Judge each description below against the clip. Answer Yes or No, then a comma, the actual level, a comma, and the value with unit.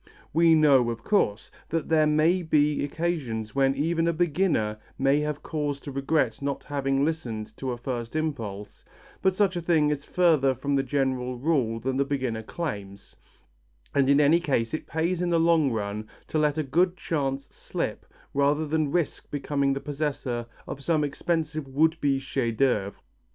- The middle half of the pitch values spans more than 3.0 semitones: Yes, average, 3.4 semitones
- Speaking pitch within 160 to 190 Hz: No, medium, 145 Hz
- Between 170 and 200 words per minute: Yes, average, 175 wpm